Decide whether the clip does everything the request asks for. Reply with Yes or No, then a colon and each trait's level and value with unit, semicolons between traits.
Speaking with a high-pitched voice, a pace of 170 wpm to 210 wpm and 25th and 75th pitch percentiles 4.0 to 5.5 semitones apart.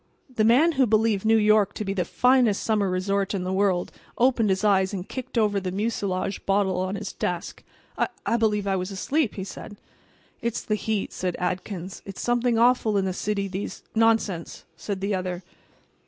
No: high, 200 Hz; average, 185 wpm; average, 2.8 semitones